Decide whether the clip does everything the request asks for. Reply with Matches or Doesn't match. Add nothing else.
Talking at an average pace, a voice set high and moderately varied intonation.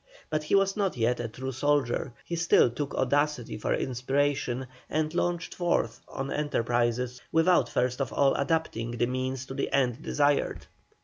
Doesn't match